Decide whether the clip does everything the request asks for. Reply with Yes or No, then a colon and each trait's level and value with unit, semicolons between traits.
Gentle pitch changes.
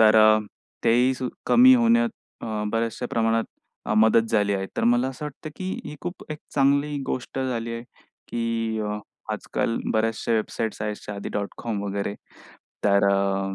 No: average, 3.6 semitones